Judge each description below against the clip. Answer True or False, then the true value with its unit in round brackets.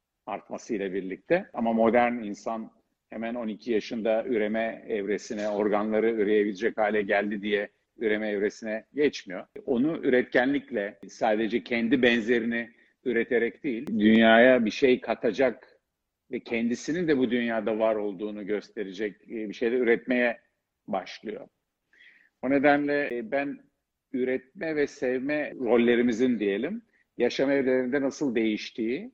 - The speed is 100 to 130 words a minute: True (110 wpm)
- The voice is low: True (115 Hz)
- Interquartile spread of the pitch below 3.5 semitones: True (2.9 semitones)